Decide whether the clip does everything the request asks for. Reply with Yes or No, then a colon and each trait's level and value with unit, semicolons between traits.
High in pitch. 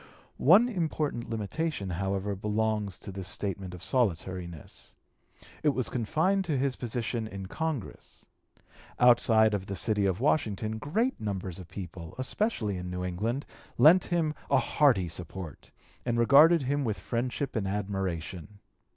No: low, 110 Hz